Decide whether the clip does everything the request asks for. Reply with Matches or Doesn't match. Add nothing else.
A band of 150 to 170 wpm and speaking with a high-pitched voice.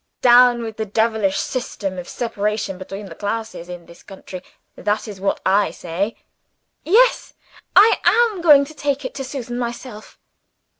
Matches